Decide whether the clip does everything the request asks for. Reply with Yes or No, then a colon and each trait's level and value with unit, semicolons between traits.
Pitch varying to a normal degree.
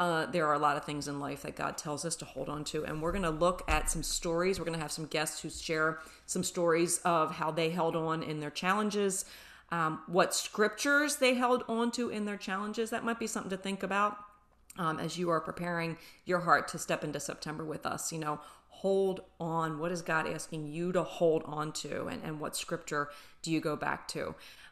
Yes: average, 3.4 semitones